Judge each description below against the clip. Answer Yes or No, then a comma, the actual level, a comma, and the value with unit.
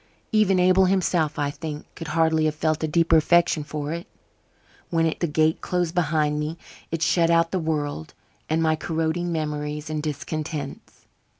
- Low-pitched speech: No, medium, 160 Hz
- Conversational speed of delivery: Yes, average, 165 wpm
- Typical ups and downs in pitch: No, narrow, 1.9 semitones